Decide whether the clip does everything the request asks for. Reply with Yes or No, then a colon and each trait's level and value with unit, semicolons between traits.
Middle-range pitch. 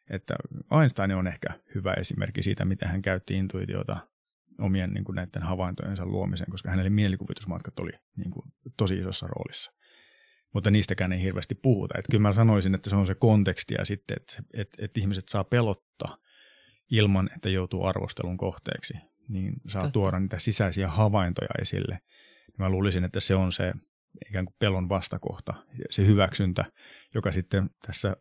No: very low, 95 Hz